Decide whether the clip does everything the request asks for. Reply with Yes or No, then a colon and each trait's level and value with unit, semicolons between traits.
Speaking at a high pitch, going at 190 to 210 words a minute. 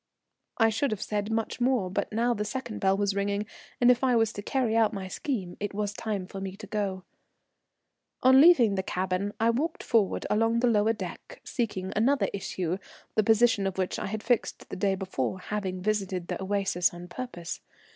Yes: high, 210 Hz; average, 195 wpm